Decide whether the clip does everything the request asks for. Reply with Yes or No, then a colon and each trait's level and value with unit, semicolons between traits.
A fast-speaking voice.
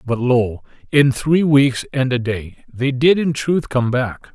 No: average, 195 wpm